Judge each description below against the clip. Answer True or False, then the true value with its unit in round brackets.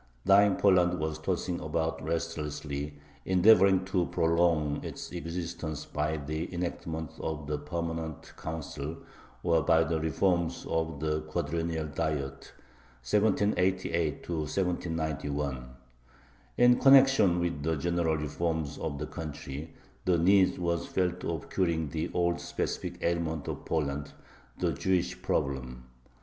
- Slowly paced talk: True (120 wpm)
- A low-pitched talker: True (80 Hz)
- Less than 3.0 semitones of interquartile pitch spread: True (2.5 semitones)